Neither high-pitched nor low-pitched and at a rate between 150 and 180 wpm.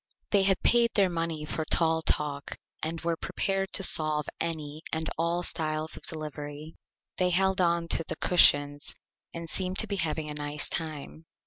Yes: medium, 160 Hz; average, 175 wpm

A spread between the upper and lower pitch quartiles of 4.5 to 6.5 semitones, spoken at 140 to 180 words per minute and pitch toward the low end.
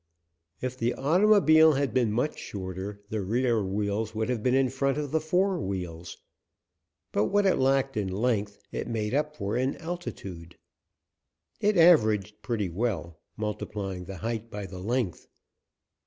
Yes: wide, 5.4 semitones; average, 150 wpm; low, 115 Hz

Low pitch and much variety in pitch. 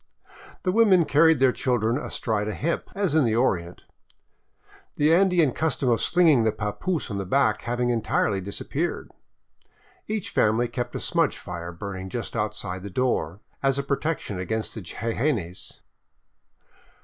Yes: low, 120 Hz; wide, 6.8 semitones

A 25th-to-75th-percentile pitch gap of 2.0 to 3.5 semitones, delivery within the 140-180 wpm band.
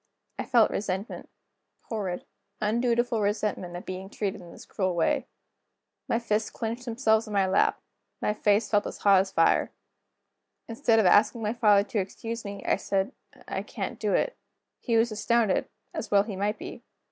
Yes: narrow, 2.6 semitones; average, 170 wpm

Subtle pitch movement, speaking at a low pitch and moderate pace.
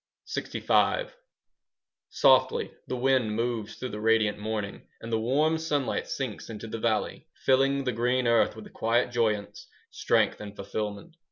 No: average, 3.4 semitones; low, 115 Hz; average, 150 wpm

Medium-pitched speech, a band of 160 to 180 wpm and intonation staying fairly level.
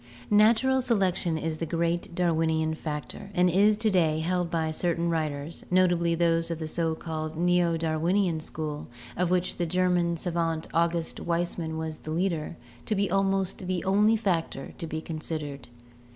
Yes: medium, 170 Hz; average, 165 wpm; narrow, 2.3 semitones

